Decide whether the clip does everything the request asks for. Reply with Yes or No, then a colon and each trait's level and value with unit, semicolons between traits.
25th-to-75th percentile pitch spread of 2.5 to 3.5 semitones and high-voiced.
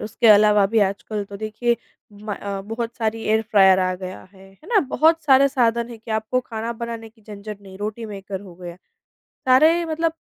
Yes: average, 2.8 semitones; high, 220 Hz